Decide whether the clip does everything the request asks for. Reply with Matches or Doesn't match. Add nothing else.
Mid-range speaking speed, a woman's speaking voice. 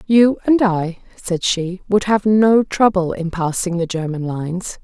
Matches